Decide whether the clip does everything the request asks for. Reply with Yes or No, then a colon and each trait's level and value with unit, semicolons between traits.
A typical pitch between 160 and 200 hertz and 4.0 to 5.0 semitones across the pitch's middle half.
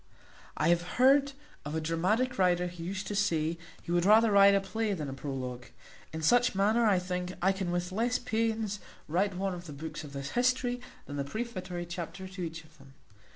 Yes: medium, 185 Hz; average, 4.6 semitones